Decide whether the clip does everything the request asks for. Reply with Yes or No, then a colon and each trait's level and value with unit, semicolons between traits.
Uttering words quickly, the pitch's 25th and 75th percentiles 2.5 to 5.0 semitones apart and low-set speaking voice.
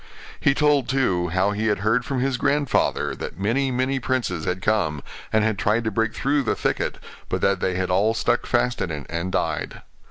No: fast, 210 wpm; wide, 5.6 semitones; low, 110 Hz